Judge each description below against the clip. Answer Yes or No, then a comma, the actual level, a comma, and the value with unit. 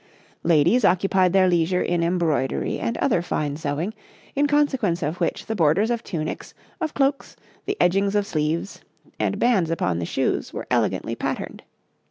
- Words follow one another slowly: No, average, 160 wpm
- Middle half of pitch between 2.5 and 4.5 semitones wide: No, wide, 5.4 semitones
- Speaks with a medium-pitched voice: Yes, medium, 180 Hz